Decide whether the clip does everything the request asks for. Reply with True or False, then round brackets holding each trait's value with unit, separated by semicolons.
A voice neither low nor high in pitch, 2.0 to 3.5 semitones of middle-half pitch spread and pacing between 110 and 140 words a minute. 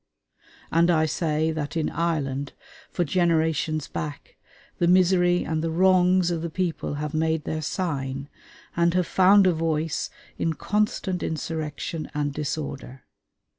True (160 Hz; 2.7 semitones; 135 wpm)